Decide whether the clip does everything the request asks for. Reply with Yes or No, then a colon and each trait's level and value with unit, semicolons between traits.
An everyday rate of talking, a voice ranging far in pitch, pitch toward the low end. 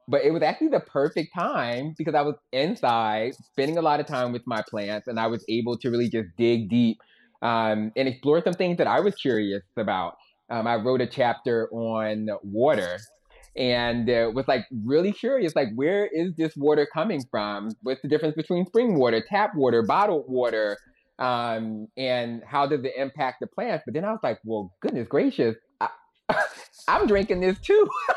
Yes: average, 190 wpm; wide, 5.9 semitones; low, 130 Hz